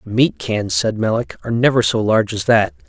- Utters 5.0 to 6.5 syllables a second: Yes, 5.4 syllables/s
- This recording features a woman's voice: No, male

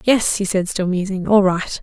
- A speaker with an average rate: No, fast, 230 wpm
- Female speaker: Yes, female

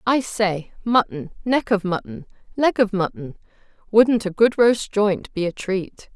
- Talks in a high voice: Yes, high, 205 Hz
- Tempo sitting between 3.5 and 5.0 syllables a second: Yes, 4.1 syllables/s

